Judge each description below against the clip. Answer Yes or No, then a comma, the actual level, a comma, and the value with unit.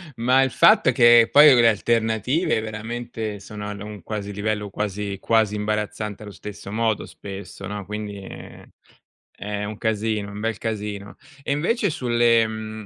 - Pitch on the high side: No, low, 110 Hz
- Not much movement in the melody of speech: Yes, narrow, 2.0 semitones